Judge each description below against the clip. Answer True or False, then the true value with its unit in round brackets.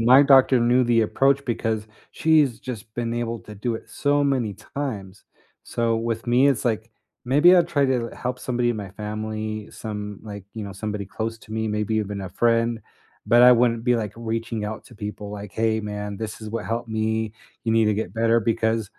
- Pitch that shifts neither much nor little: False (2.1 semitones)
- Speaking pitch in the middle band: False (115 Hz)